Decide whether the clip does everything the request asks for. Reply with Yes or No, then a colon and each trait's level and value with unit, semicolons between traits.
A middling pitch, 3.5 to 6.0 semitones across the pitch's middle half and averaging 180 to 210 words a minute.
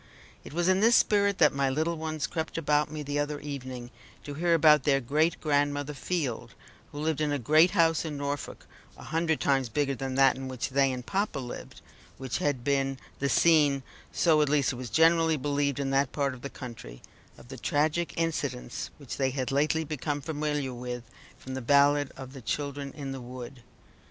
No: medium, 145 Hz; narrow, 2.6 semitones; average, 200 wpm